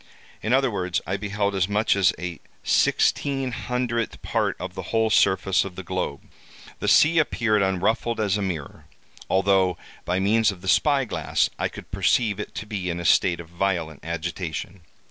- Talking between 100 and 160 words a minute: No, average, 180 wpm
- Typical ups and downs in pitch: Yes, average, 3.5 semitones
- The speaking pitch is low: Yes, very low, 95 Hz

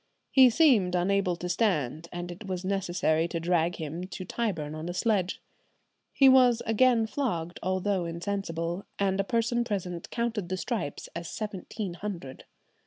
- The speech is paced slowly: No, average, 155 wpm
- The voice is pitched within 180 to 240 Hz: Yes, medium, 185 Hz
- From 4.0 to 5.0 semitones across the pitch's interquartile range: Yes, average, 4.3 semitones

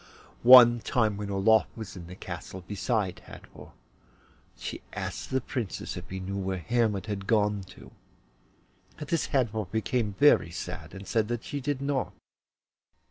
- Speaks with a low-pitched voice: Yes, low, 110 Hz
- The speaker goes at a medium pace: Yes, average, 155 wpm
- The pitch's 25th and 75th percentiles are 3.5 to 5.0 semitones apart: Yes, average, 3.9 semitones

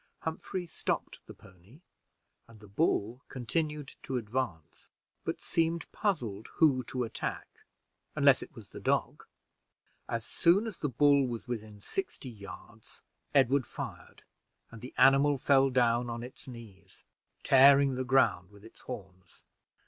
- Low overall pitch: Yes, low, 125 Hz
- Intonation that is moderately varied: Yes, average, 4.3 semitones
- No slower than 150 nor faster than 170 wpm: No, average, 140 wpm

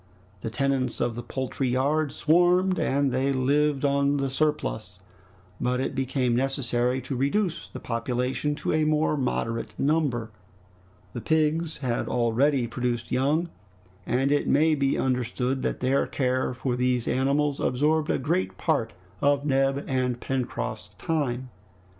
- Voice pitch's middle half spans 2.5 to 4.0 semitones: Yes, average, 2.9 semitones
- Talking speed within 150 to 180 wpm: No, average, 140 wpm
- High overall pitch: No, low, 135 Hz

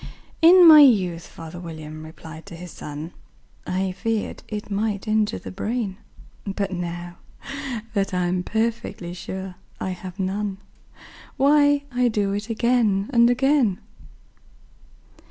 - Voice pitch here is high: Yes, high, 195 Hz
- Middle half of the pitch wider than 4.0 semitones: Yes, average, 4.4 semitones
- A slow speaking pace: Yes, slow, 125 wpm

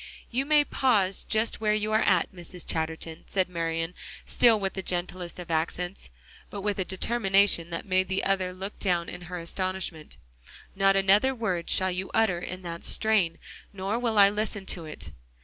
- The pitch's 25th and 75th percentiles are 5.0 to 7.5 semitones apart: No, average, 3.0 semitones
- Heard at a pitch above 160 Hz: Yes, high, 190 Hz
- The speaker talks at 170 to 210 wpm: Yes, average, 180 wpm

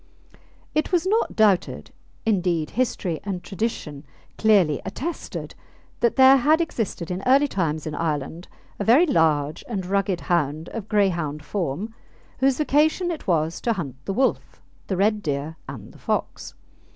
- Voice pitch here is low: No, high, 195 Hz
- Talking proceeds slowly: No, average, 150 wpm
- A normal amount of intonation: No, wide, 7.3 semitones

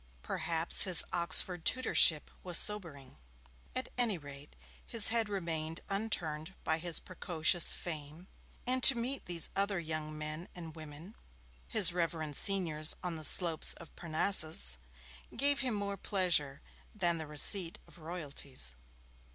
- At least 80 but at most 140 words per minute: Yes, slow, 135 wpm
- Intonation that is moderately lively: Yes, average, 4.1 semitones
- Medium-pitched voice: Yes, medium, 170 Hz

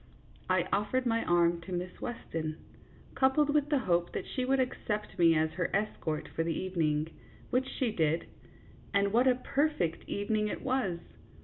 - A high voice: Yes, high, 200 Hz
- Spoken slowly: No, average, 180 wpm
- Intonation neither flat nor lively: No, wide, 7.1 semitones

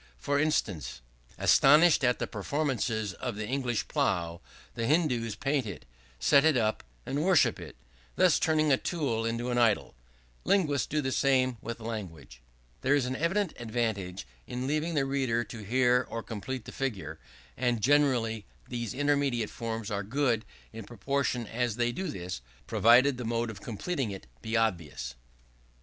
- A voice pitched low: Yes, low, 120 Hz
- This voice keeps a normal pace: Yes, average, 160 wpm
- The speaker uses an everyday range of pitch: Yes, average, 4.2 semitones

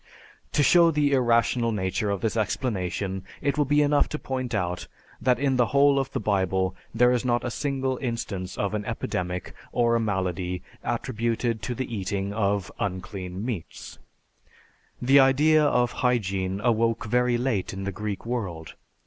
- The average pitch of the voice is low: Yes, low, 115 Hz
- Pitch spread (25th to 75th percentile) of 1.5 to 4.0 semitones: No, average, 4.9 semitones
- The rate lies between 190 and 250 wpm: No, average, 165 wpm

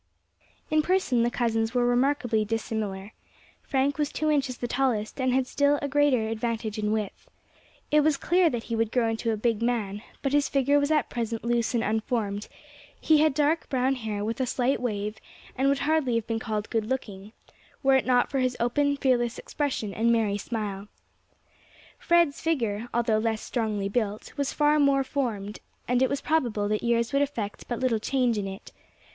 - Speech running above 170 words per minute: Yes, average, 190 wpm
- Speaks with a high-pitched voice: Yes, high, 240 Hz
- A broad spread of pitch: No, average, 4.0 semitones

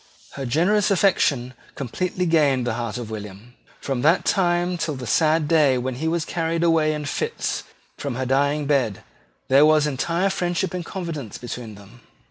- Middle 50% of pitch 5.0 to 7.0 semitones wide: Yes, average, 5.3 semitones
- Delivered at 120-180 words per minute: Yes, average, 170 wpm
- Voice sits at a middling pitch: Yes, medium, 150 Hz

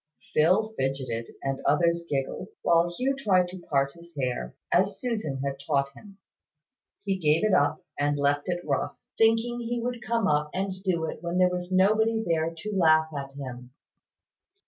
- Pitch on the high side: No, medium, 170 Hz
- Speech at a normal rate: Yes, average, 170 wpm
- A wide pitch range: Yes, wide, 5.7 semitones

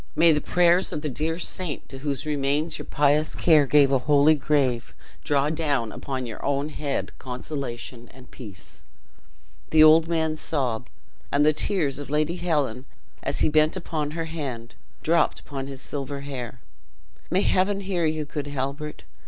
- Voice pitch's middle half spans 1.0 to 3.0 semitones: Yes, narrow, 2.6 semitones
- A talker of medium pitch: Yes, medium, 145 Hz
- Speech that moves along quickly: No, average, 165 wpm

